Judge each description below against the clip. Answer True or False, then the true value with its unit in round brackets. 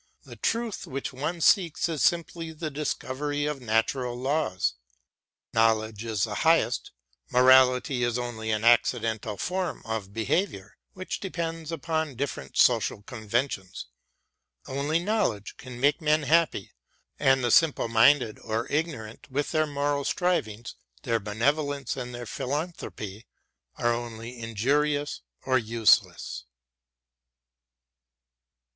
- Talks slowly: True (115 wpm)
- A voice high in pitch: False (130 Hz)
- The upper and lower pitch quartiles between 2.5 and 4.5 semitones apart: False (5.1 semitones)